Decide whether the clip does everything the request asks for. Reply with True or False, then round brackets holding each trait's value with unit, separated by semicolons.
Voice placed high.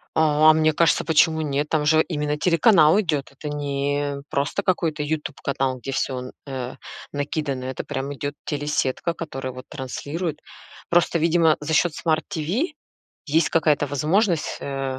False (150 Hz)